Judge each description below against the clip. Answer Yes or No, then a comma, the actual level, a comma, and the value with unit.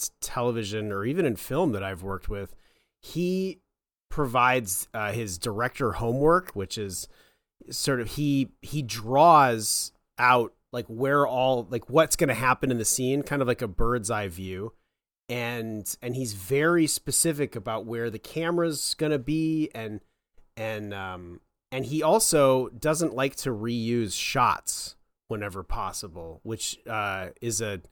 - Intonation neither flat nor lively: Yes, average, 4.6 semitones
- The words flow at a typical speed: Yes, average, 150 wpm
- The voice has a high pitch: No, low, 120 Hz